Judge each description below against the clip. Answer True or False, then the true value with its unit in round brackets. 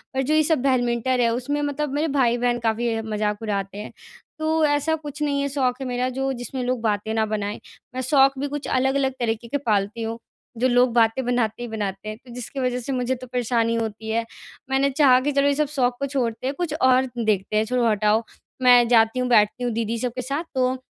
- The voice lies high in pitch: True (245 Hz)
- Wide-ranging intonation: False (3.1 semitones)